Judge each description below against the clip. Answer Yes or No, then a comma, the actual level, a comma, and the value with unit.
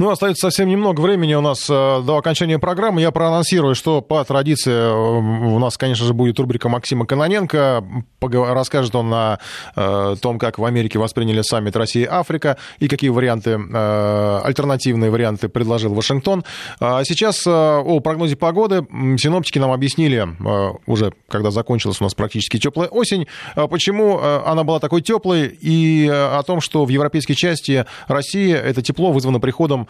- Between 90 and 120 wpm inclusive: No, average, 150 wpm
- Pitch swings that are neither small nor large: No, wide, 5.7 semitones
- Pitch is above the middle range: No, medium, 140 Hz